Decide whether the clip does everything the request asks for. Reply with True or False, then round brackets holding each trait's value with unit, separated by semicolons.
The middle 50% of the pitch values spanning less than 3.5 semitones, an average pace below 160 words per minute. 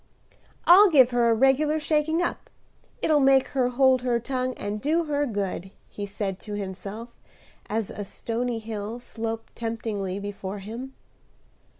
False (4.5 semitones; 150 wpm)